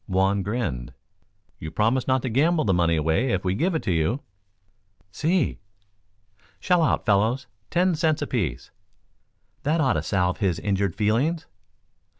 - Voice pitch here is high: No, low, 110 Hz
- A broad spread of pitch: Yes, wide, 7.9 semitones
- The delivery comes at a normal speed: Yes, average, 150 wpm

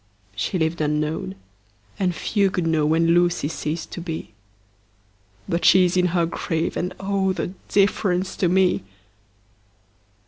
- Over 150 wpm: No, average, 145 wpm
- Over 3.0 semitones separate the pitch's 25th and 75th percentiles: No, narrow, 2.4 semitones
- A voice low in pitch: No, medium, 175 Hz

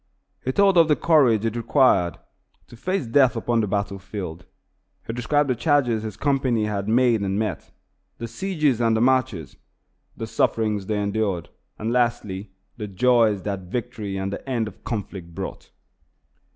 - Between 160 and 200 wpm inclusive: Yes, average, 165 wpm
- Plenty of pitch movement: No, average, 3.9 semitones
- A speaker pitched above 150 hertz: No, low, 115 Hz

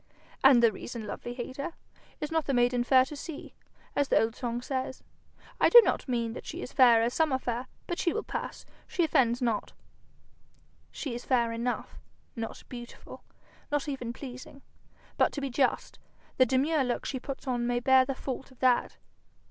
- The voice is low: No, very high, 255 Hz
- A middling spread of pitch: No, narrow, 2.3 semitones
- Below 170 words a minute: No, average, 190 wpm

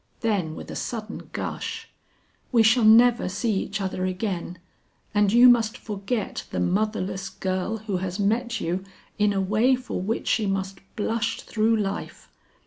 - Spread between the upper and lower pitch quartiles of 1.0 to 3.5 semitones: Yes, average, 2.9 semitones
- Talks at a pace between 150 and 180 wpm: Yes, average, 155 wpm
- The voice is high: Yes, high, 210 Hz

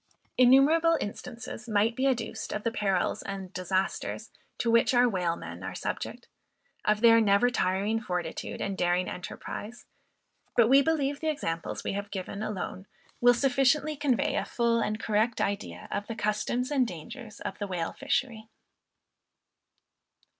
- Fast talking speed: No, average, 145 wpm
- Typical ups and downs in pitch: Yes, average, 4.1 semitones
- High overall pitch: Yes, high, 225 Hz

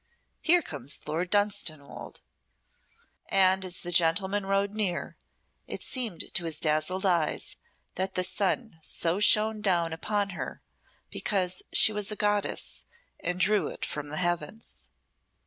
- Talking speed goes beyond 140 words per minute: No, slow, 135 wpm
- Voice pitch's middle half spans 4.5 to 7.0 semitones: No, average, 3.6 semitones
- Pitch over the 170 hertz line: Yes, medium, 185 Hz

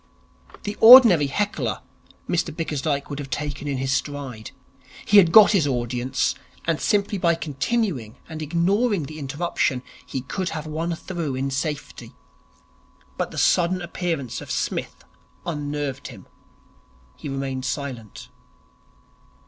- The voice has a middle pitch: Yes, medium, 150 Hz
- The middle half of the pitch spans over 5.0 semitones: No, average, 4.3 semitones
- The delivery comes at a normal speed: No, slow, 130 wpm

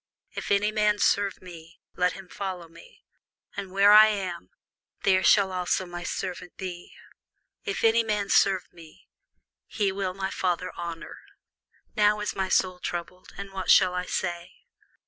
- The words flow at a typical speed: Yes, average, 155 wpm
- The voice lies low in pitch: No, high, 190 Hz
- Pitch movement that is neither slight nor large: No, narrow, 2.1 semitones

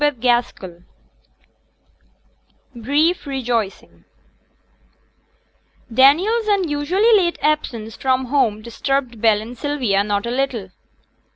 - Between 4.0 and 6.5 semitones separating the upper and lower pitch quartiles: Yes, average, 4.6 semitones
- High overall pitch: Yes, very high, 260 Hz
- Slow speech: Yes, slow, 90 wpm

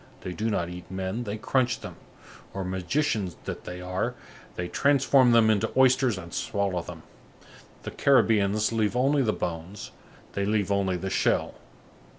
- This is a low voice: Yes, low, 100 Hz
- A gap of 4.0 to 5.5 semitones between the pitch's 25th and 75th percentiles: Yes, average, 4.6 semitones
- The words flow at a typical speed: Yes, average, 160 wpm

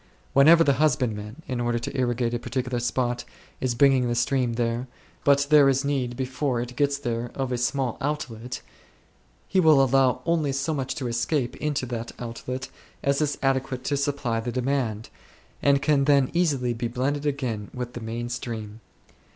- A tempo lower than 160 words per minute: No, average, 175 wpm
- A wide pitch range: No, average, 2.7 semitones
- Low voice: Yes, low, 130 Hz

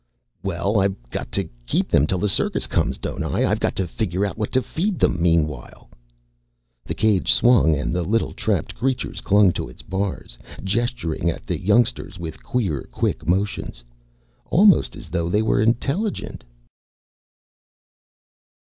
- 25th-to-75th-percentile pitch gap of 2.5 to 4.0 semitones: No, average, 5.1 semitones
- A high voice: No, low, 100 Hz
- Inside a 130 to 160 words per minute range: Yes, average, 155 wpm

